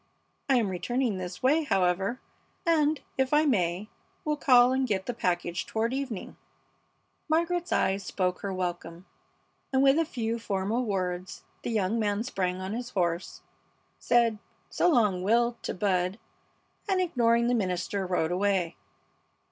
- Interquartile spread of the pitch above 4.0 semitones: Yes, wide, 5.6 semitones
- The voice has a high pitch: Yes, high, 215 Hz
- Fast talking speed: No, average, 150 wpm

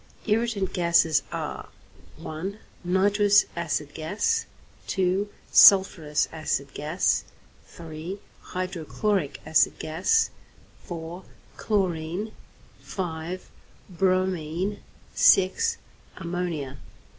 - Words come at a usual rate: No, slow, 75 wpm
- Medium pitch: Yes, medium, 180 Hz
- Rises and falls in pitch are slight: No, average, 3.5 semitones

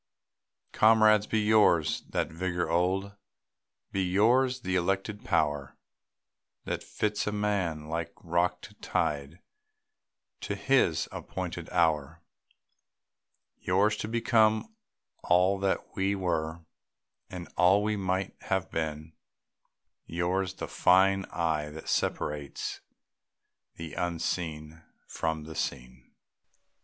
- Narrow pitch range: No, average, 3.9 semitones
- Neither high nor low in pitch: No, very low, 90 Hz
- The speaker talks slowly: Yes, slow, 105 wpm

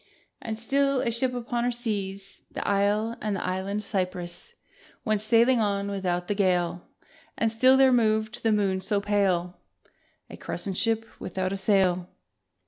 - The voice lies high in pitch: Yes, high, 205 Hz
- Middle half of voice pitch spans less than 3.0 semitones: No, average, 3.3 semitones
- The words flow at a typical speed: Yes, average, 155 wpm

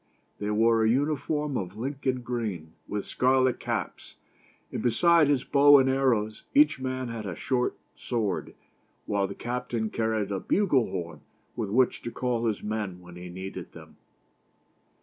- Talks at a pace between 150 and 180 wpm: Yes, average, 160 wpm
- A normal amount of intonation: Yes, average, 4.2 semitones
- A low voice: Yes, low, 115 Hz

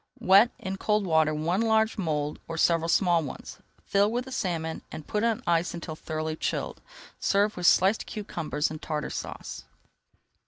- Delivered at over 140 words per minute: Yes, average, 165 wpm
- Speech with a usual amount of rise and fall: Yes, average, 4.7 semitones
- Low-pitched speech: No, medium, 175 Hz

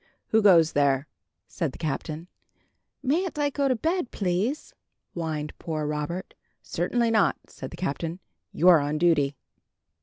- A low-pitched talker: No, medium, 170 Hz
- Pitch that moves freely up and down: Yes, wide, 6.8 semitones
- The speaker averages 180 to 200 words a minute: No, average, 140 wpm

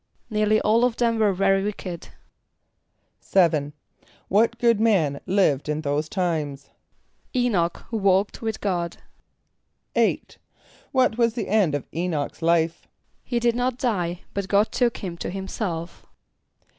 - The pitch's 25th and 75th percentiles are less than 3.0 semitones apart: No, average, 4.9 semitones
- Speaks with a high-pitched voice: Yes, high, 195 Hz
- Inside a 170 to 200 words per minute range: No, slow, 135 wpm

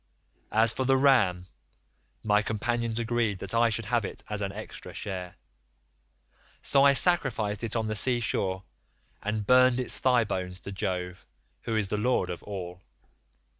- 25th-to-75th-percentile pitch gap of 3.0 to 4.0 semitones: Yes, average, 3.5 semitones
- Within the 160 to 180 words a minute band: Yes, average, 165 wpm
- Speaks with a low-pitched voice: Yes, low, 110 Hz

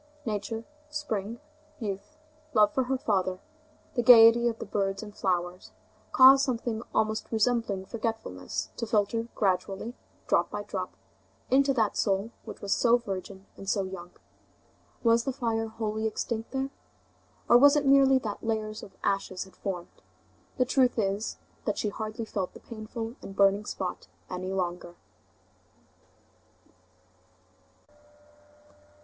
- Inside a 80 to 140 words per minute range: Yes, slow, 135 wpm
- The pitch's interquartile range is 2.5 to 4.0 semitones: Yes, average, 3.3 semitones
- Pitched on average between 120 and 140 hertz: No, high, 220 Hz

